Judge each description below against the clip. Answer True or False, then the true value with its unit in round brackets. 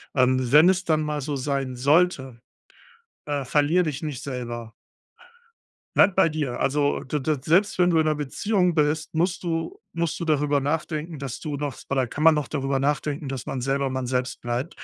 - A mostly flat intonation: False (3.2 semitones)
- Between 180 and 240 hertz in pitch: False (145 Hz)